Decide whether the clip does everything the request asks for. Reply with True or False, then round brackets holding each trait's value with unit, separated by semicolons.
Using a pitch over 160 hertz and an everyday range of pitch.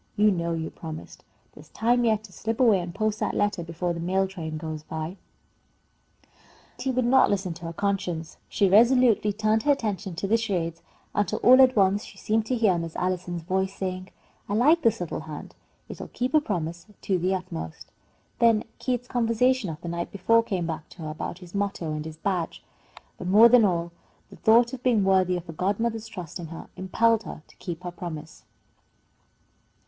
True (190 Hz; 4.7 semitones)